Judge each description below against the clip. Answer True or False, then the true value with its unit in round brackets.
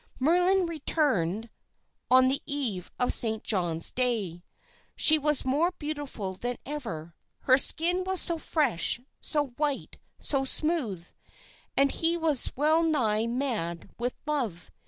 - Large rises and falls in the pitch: True (6.0 semitones)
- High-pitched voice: True (270 Hz)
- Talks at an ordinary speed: False (130 wpm)